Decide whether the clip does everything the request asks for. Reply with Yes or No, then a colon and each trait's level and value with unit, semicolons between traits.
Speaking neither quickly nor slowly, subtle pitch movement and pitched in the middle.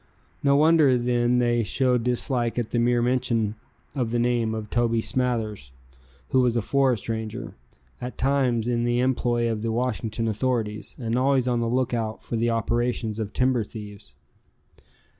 No: average, 160 wpm; narrow, 1.8 semitones; low, 120 Hz